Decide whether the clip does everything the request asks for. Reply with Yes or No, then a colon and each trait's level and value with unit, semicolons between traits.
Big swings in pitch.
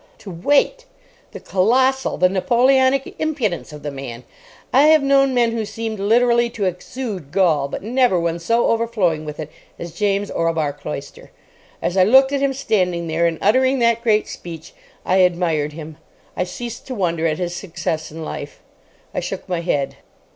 Yes: wide, 6.6 semitones